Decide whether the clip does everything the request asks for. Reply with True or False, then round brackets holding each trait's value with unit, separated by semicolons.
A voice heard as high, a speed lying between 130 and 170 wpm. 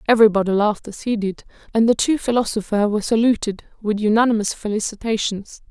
True (215 Hz; 145 wpm)